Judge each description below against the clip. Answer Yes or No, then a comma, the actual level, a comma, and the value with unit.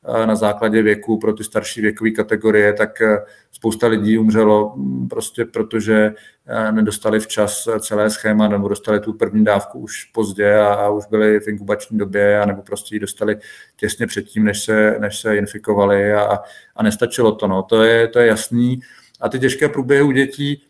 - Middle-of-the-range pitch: No, low, 105 Hz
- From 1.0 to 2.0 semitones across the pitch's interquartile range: Yes, narrow, 1.3 semitones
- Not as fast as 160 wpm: No, fast, 170 wpm